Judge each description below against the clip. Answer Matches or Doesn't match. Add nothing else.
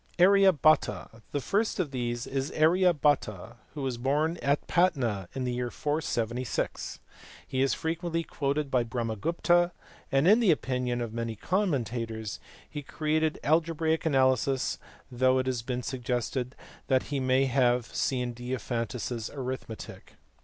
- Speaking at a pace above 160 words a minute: Doesn't match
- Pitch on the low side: Matches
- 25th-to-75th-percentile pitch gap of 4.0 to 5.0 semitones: Matches